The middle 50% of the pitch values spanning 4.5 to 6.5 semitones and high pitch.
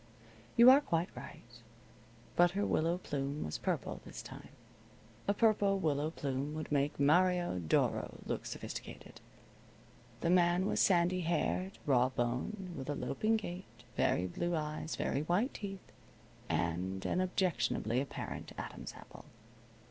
No: average, 5.3 semitones; medium, 165 Hz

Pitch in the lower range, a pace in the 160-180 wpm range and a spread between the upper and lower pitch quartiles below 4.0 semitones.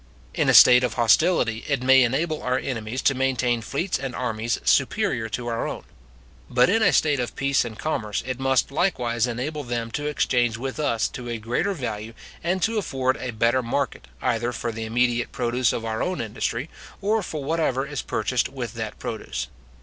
No: low, 125 Hz; average, 190 wpm; average, 3.1 semitones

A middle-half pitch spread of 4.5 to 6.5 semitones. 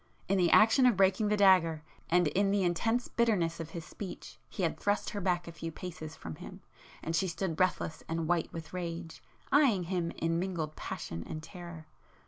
No: average, 3.0 semitones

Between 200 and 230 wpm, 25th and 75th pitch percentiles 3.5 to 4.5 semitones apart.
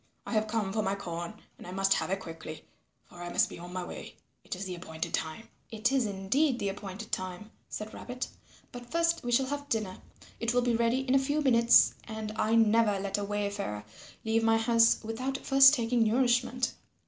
Yes: fast, 205 wpm; average, 4.0 semitones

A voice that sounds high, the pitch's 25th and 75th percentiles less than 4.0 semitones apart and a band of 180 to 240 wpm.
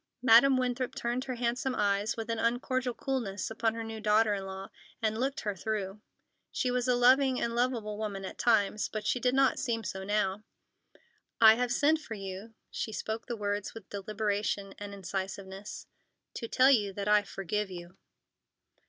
No: high, 220 Hz; average, 3.3 semitones; average, 170 wpm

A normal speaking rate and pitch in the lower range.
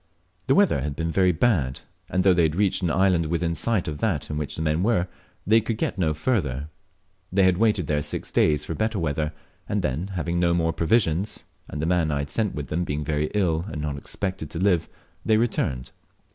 No: fast, 220 wpm; very low, 85 Hz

